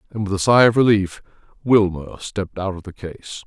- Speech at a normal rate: No, fast, 210 wpm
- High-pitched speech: No, low, 100 Hz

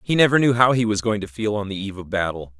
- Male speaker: Yes, male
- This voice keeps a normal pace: No, fast, 325 wpm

